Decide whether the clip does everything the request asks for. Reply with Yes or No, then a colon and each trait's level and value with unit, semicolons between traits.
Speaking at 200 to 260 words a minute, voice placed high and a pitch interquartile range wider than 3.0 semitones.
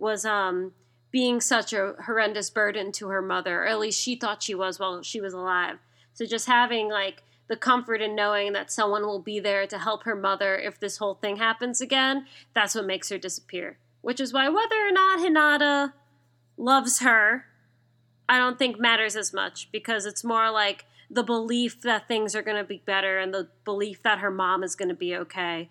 Yes: fast, 205 wpm; high, 210 Hz; average, 3.4 semitones